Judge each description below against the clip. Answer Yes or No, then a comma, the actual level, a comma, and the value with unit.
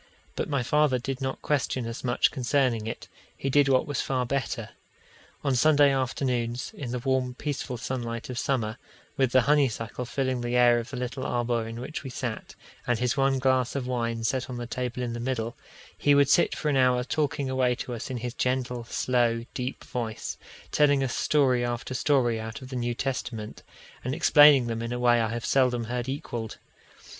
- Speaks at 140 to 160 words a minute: No, average, 200 wpm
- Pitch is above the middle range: No, low, 125 Hz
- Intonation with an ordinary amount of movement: No, narrow, 2.1 semitones